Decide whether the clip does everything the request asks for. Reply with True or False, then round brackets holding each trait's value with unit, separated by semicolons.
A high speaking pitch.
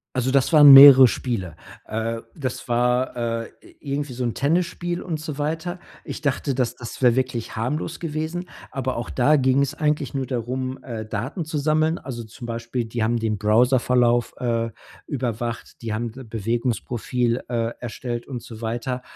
False (125 Hz)